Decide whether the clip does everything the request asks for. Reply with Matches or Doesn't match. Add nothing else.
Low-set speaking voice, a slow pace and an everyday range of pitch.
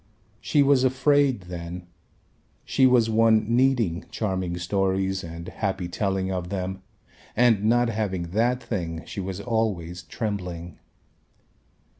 Matches